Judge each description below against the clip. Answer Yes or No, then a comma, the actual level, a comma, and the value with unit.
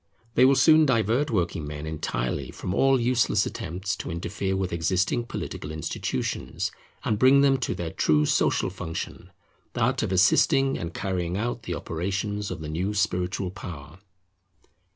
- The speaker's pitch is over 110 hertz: No, very low, 95 Hz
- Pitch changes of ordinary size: No, wide, 5.8 semitones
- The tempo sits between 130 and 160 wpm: Yes, average, 150 wpm